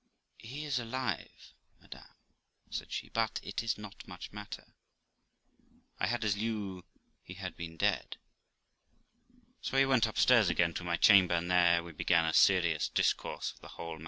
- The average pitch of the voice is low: Yes, low, 100 Hz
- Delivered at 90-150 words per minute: No, average, 165 wpm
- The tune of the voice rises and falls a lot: No, average, 4.8 semitones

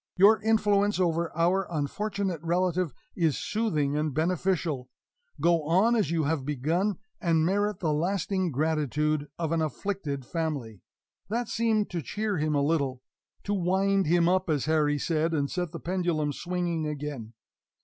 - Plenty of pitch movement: No, average, 4.0 semitones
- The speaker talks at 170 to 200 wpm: No, average, 150 wpm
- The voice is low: No, medium, 170 Hz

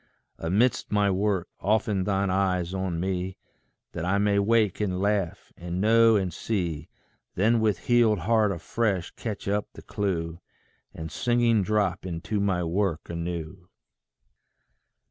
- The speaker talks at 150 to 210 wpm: No, slow, 135 wpm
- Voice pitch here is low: Yes, very low, 95 Hz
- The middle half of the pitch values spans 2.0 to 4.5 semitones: Yes, average, 3.2 semitones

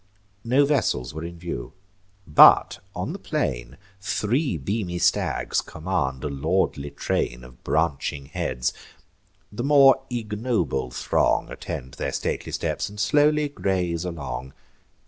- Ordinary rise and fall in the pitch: No, wide, 8.4 semitones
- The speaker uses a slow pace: Yes, slow, 125 wpm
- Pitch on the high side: No, very low, 85 Hz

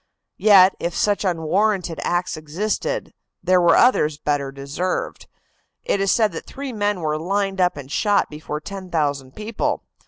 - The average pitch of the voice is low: No, medium, 180 Hz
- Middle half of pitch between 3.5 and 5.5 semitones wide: Yes, average, 4.9 semitones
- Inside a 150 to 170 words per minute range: Yes, average, 155 wpm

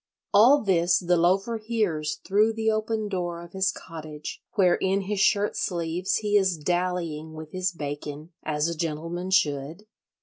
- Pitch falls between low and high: Yes, medium, 180 Hz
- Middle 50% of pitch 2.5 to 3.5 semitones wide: No, average, 4.0 semitones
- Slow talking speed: No, average, 160 wpm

